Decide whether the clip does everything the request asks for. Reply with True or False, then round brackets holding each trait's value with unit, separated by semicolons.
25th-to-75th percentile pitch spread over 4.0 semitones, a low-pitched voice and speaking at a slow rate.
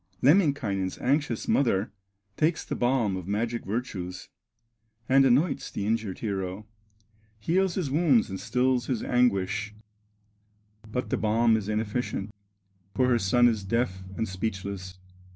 True (4.4 semitones; 115 Hz; 130 wpm)